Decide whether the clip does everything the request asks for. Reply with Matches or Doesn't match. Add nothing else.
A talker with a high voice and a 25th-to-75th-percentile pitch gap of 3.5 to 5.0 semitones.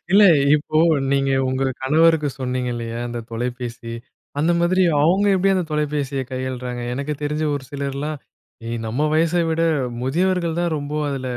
Doesn't match